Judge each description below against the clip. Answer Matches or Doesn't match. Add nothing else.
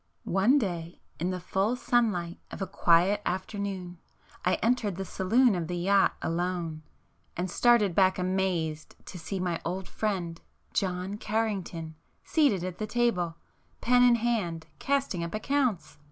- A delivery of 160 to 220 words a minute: Doesn't match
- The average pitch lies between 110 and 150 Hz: Doesn't match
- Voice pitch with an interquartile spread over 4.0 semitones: Doesn't match